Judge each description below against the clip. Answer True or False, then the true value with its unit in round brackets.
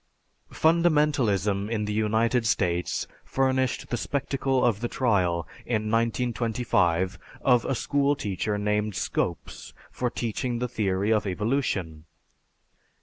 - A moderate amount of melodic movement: True (3.7 semitones)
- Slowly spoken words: True (115 wpm)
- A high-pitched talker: False (110 Hz)